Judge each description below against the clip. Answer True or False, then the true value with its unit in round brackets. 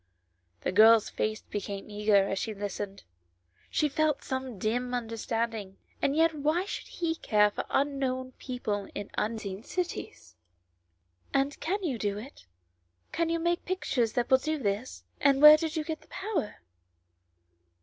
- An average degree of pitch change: False (6.7 semitones)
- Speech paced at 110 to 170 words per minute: True (160 wpm)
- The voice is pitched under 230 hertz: False (245 Hz)